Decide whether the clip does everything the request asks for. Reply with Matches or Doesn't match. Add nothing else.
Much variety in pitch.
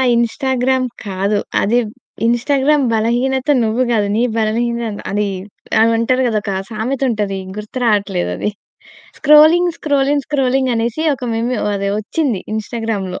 Doesn't match